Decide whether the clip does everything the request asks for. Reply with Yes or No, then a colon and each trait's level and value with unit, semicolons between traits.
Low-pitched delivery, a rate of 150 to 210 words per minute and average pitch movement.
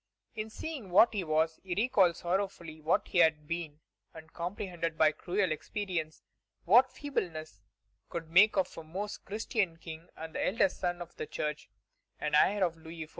No: medium, 175 Hz; average, 170 wpm; average, 3.8 semitones